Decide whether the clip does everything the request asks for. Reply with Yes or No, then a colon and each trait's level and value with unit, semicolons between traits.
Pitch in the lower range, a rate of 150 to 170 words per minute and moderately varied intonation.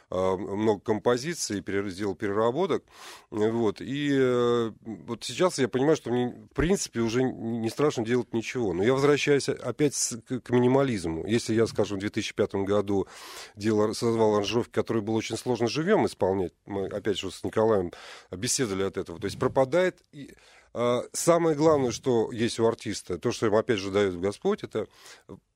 Yes: low, 115 Hz; average, 155 wpm; average, 3.7 semitones